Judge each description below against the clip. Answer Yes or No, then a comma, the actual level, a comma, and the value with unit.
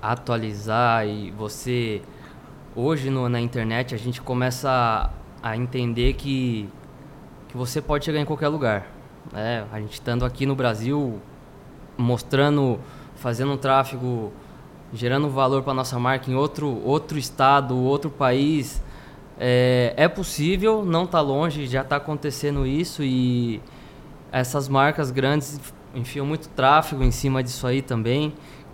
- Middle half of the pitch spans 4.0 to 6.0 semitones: No, average, 2.9 semitones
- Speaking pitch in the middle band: No, low, 130 Hz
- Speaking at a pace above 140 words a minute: No, average, 135 wpm